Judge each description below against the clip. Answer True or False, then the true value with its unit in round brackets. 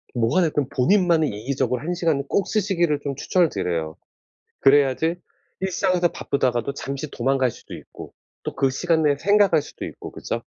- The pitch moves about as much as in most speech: True (4.9 semitones)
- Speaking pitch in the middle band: True (145 Hz)